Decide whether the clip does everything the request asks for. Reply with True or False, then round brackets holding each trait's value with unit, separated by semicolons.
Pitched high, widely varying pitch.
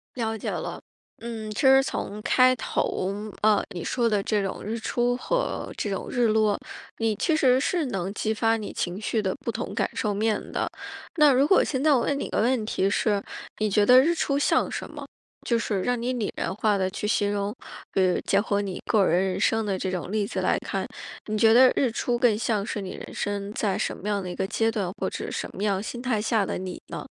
False (215 Hz; 3.3 semitones)